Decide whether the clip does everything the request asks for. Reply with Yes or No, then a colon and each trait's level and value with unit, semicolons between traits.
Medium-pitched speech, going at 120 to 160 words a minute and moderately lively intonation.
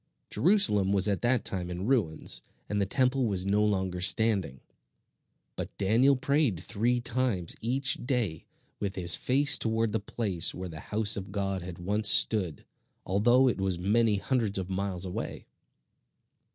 No: low, 100 Hz; average, 155 wpm; average, 4.2 semitones